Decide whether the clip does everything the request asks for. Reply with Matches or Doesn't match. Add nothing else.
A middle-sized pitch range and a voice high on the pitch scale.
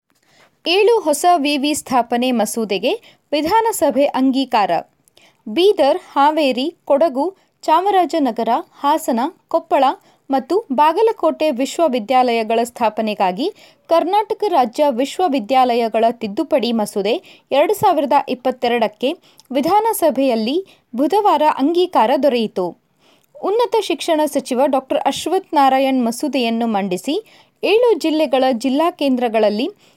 Matches